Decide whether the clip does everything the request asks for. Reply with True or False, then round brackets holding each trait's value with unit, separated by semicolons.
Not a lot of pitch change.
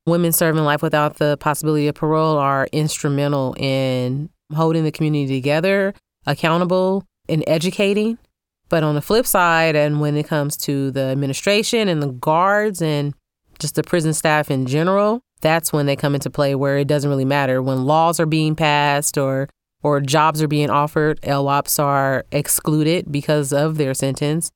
True (2.2 semitones)